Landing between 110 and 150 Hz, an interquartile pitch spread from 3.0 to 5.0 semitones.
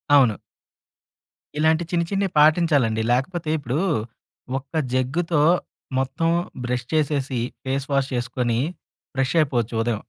Yes: low, 135 Hz; average, 4.1 semitones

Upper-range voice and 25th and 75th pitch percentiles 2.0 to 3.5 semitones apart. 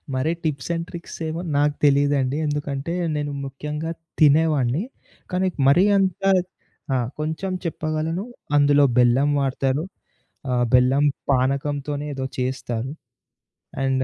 No: medium, 145 Hz; average, 2.8 semitones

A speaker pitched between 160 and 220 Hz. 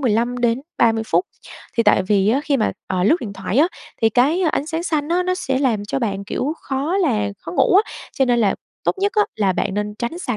No: high, 245 Hz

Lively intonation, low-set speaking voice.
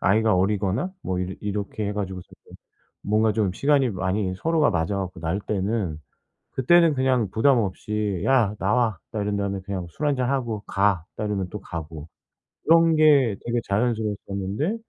No: average, 4.3 semitones; low, 105 Hz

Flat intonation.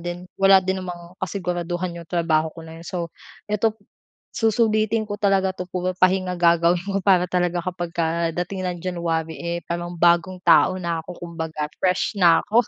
Yes: narrow, 1.8 semitones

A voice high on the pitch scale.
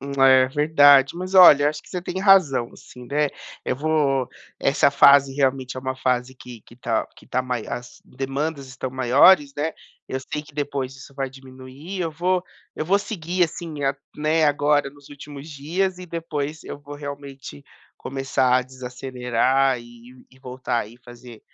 No: medium, 140 Hz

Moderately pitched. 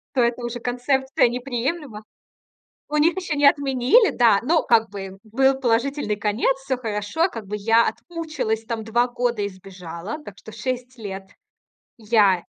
No: high, 240 Hz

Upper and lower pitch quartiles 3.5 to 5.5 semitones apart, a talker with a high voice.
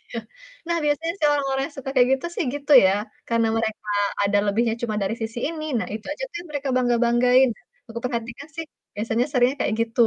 Yes: average, 4.0 semitones; high, 245 Hz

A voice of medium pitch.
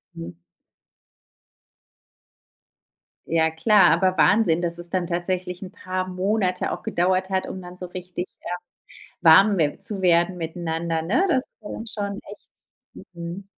Yes: medium, 180 Hz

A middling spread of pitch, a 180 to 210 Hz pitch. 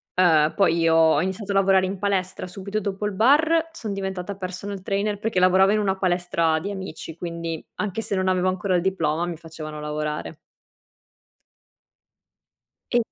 Yes: average, 3.0 semitones; medium, 185 Hz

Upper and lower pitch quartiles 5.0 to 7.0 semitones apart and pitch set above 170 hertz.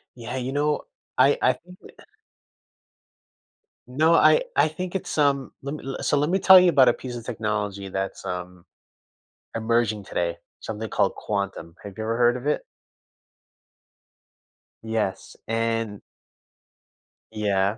No: wide, 5.5 semitones; low, 115 Hz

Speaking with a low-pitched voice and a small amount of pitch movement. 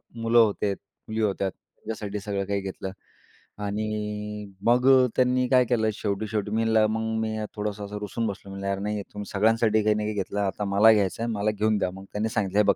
Yes: low, 105 Hz; narrow, 1.6 semitones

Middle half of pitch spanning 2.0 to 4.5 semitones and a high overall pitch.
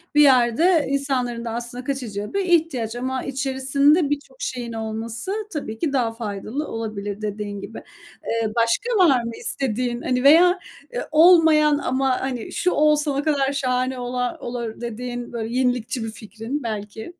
Yes: average, 3.9 semitones; very high, 250 Hz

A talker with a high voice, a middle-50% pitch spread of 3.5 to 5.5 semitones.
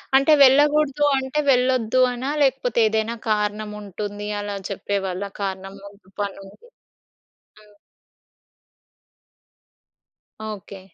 Yes: high, 215 Hz; average, 4.5 semitones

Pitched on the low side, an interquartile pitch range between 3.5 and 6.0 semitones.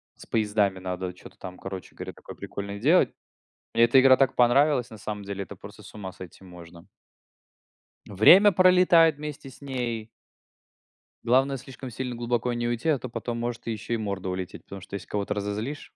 Yes: low, 115 Hz; average, 5.0 semitones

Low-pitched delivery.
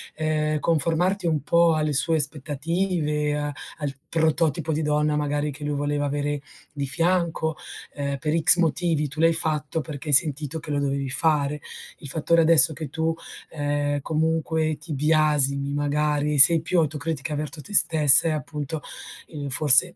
No: medium, 150 Hz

